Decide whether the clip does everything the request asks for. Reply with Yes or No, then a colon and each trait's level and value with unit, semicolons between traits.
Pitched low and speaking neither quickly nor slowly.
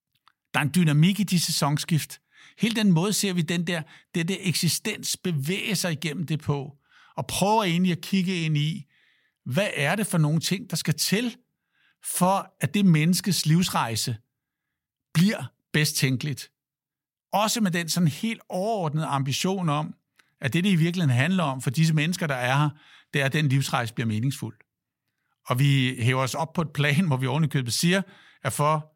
No: medium, 160 Hz; average, 185 wpm